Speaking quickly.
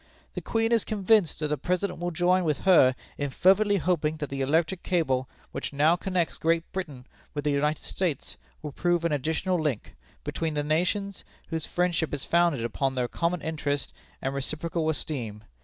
No: average, 175 wpm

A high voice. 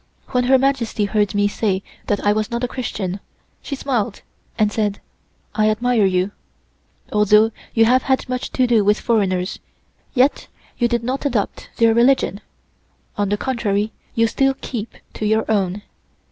Yes: high, 220 Hz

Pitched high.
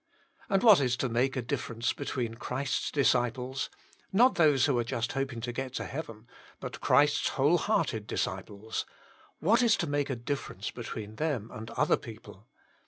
No: low, 130 Hz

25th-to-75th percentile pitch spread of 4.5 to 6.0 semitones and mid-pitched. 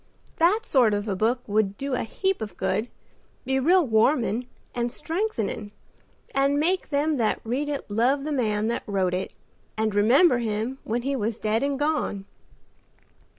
No: average, 4.9 semitones; high, 240 Hz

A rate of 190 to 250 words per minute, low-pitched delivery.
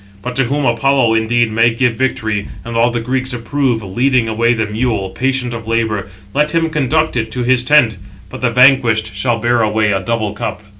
Yes: average, 200 wpm; low, 120 Hz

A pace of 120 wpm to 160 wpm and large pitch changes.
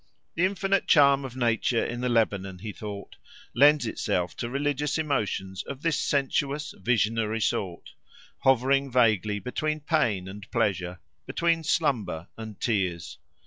Yes: slow, 135 wpm; wide, 5.9 semitones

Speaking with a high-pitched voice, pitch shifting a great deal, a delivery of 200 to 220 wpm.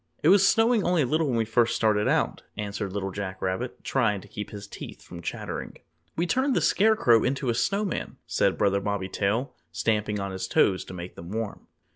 No: low, 105 Hz; wide, 7.2 semitones; fast, 205 wpm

